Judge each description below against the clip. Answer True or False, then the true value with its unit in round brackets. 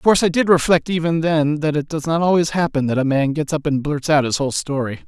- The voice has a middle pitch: True (155 Hz)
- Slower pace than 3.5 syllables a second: False (6.2 syllables/s)